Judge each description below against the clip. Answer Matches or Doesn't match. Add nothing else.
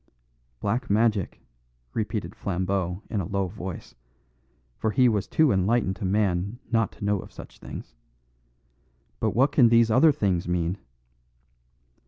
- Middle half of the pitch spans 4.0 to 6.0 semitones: Doesn't match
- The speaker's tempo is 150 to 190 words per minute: Doesn't match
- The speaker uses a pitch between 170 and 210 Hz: Doesn't match